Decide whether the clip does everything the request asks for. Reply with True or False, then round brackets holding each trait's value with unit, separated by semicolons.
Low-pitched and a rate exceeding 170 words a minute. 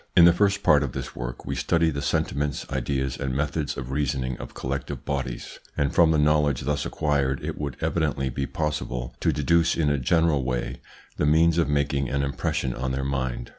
True (70 Hz; 200 wpm)